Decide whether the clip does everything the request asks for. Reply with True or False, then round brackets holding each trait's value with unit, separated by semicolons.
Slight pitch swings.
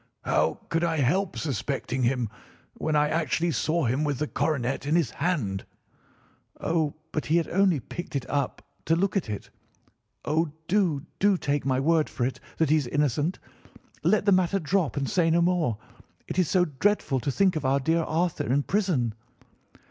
False (4.1 semitones)